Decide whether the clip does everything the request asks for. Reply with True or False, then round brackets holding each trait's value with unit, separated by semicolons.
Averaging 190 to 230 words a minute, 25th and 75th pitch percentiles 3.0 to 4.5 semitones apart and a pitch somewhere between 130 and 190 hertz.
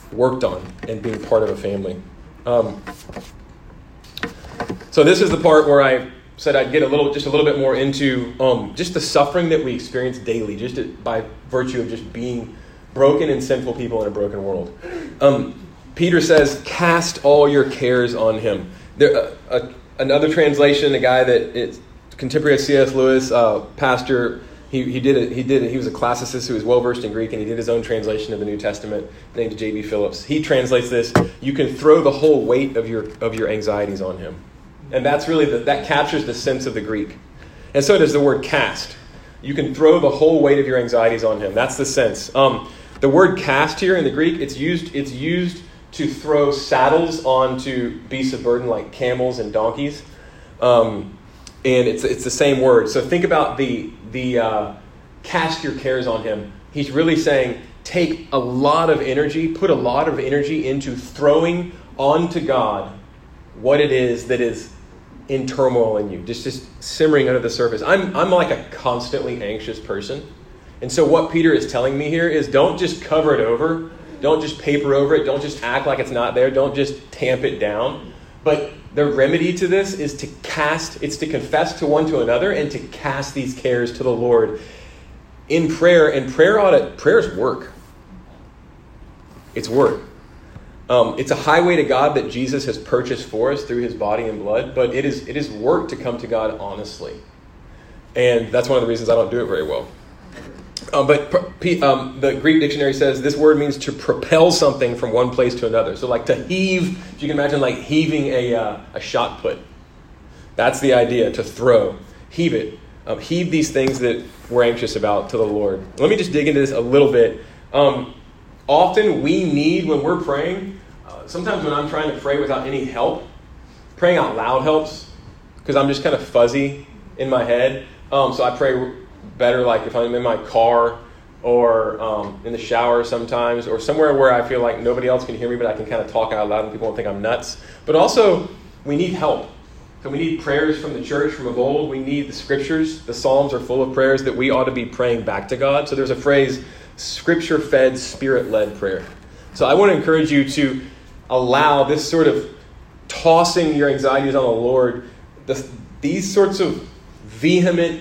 True (200 wpm; 4.2 semitones; 135 Hz)